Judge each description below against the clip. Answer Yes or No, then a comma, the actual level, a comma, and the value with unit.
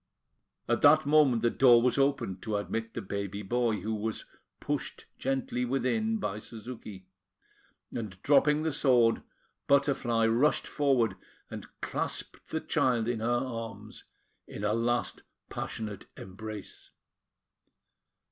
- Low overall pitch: Yes, low, 115 Hz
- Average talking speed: No, slow, 125 wpm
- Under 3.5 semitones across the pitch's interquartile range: No, average, 3.9 semitones